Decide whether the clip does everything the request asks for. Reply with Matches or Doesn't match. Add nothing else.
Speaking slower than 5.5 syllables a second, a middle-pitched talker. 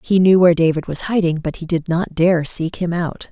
Matches